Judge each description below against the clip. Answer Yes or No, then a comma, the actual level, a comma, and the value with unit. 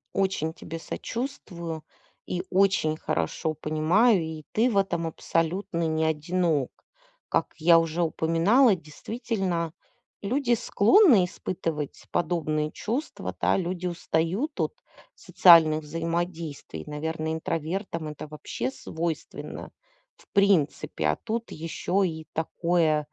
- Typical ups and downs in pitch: Yes, average, 3.4 semitones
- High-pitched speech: No, medium, 165 Hz